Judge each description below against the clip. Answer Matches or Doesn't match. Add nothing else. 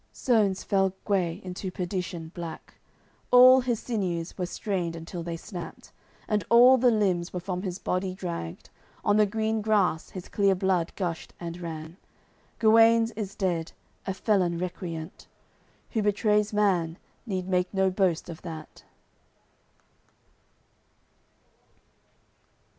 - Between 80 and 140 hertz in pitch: Doesn't match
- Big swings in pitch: Doesn't match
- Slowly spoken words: Matches